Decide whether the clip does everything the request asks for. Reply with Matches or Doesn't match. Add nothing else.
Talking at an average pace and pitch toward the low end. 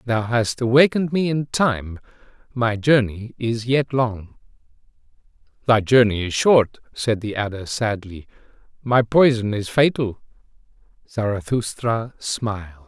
Doesn't match